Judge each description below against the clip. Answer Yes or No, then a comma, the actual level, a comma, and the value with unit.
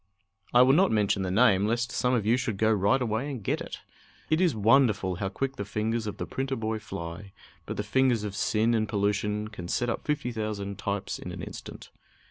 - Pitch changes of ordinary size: Yes, average, 3.4 semitones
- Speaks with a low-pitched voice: Yes, low, 110 Hz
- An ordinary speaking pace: No, fast, 220 wpm